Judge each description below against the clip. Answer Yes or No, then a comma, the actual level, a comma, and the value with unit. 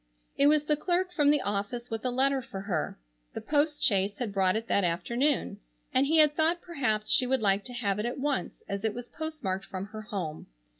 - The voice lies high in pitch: Yes, high, 240 Hz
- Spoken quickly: Yes, fast, 220 wpm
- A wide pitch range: Yes, wide, 6.5 semitones